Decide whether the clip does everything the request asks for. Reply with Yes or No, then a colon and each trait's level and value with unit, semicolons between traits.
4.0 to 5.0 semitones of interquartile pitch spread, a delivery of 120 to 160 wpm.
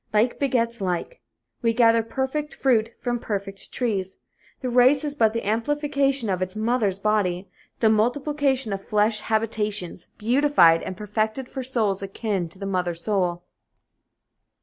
Yes: average, 4.3 semitones; average, 145 wpm